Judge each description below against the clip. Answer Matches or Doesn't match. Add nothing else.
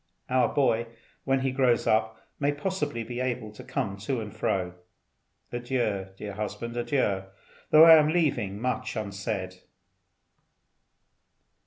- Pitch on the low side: Matches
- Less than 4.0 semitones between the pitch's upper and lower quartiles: Doesn't match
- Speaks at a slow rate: Matches